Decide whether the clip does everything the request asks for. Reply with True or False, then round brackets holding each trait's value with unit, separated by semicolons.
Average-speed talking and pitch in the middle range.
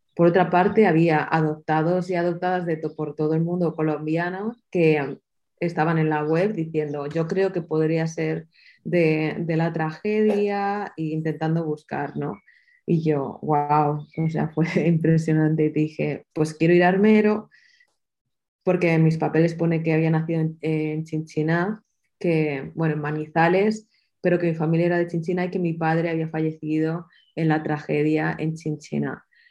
True (165 wpm; 160 Hz)